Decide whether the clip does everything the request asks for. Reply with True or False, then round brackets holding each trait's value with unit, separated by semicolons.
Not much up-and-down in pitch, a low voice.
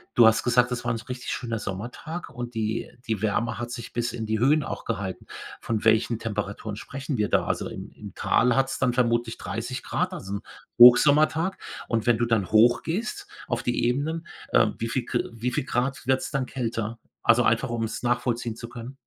True (2.3 semitones; 120 Hz)